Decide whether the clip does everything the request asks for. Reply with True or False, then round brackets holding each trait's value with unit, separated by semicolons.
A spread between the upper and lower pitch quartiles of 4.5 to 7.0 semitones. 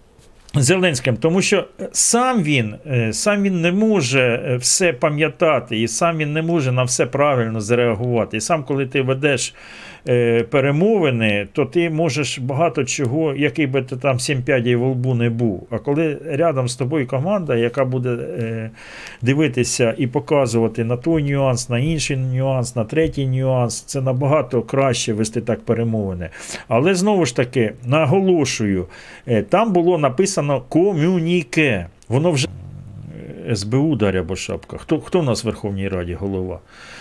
True (5.0 semitones)